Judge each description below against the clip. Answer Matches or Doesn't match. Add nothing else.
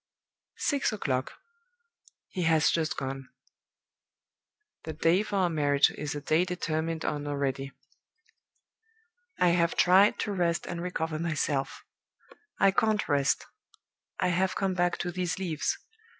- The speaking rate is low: Matches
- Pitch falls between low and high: Matches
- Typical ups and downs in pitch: Matches